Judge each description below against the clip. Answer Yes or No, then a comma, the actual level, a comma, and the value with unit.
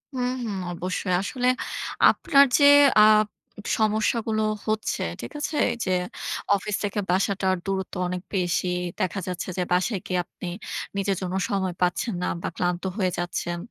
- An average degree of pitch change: Yes, average, 3.0 semitones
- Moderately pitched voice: No, high, 195 Hz